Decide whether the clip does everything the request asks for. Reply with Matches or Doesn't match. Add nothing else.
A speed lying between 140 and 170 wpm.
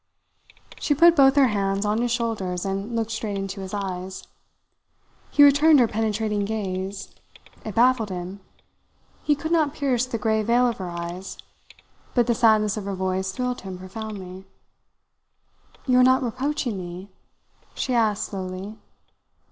Matches